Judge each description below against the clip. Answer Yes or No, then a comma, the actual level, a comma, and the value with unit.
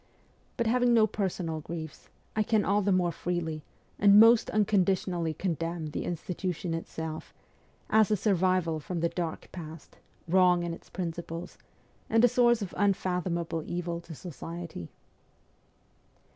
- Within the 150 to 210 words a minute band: No, slow, 135 wpm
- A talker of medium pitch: Yes, medium, 175 Hz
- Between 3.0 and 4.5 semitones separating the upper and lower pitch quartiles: Yes, average, 3.4 semitones